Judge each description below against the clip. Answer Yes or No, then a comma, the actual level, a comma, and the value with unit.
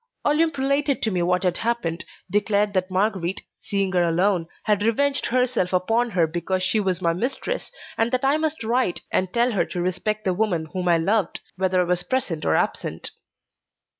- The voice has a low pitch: No, high, 195 Hz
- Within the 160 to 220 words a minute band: Yes, average, 190 wpm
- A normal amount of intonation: Yes, average, 4.8 semitones